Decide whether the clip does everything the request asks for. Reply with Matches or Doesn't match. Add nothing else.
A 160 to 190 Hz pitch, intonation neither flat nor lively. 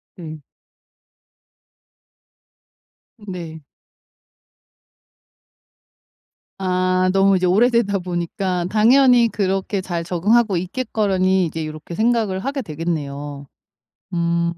Matches